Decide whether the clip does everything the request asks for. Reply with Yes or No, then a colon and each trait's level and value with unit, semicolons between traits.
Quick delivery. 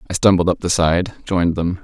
Yes: fast, 230 wpm